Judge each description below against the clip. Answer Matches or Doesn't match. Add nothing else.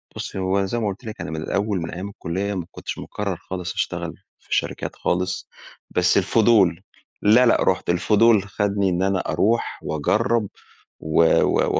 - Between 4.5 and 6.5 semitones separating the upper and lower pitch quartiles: Doesn't match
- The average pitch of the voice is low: Matches